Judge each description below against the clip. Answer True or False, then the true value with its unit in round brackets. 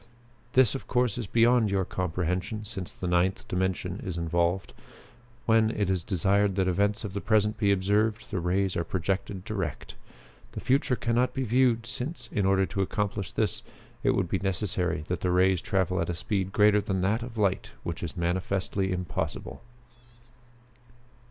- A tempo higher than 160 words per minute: True (170 wpm)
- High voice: False (95 Hz)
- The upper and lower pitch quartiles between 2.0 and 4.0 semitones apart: True (2.9 semitones)